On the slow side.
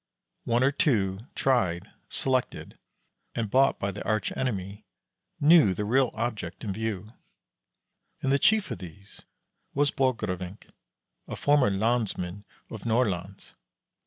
Yes: slow, 125 wpm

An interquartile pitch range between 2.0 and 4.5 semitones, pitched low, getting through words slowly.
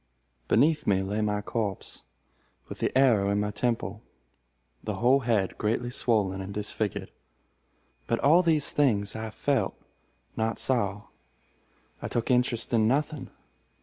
Yes: average, 3.6 semitones; low, 110 Hz; slow, 130 wpm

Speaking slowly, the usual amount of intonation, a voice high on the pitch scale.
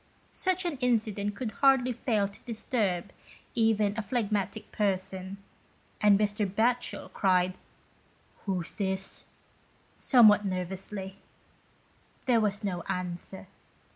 Yes: slow, 105 wpm; average, 3.0 semitones; high, 205 Hz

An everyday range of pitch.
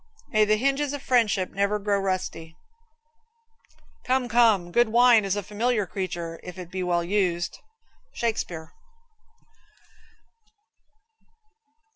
Yes: average, 4.6 semitones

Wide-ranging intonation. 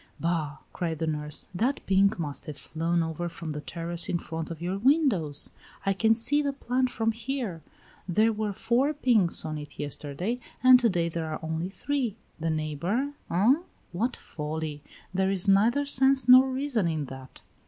Yes: wide, 7.1 semitones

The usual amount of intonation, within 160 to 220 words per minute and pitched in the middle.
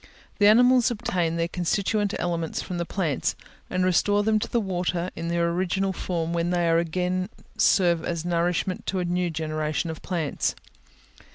No: narrow, 2.2 semitones; average, 165 wpm; medium, 175 Hz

